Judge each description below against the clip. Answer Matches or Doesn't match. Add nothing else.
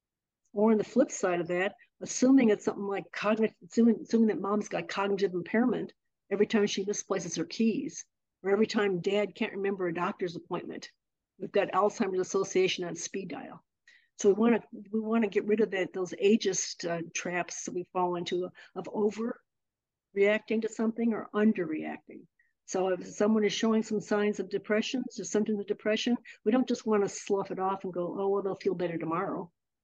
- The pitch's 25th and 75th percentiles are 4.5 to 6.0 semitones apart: Doesn't match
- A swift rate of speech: Doesn't match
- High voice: Matches